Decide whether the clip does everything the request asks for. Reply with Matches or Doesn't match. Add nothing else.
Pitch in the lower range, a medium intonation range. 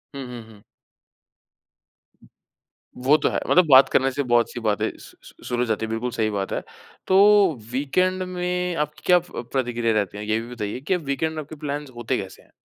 Doesn't match